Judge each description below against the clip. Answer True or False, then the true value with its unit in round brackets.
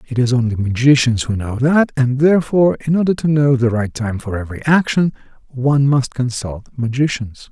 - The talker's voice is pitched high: False (130 Hz)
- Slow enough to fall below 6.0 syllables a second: True (5.6 syllables/s)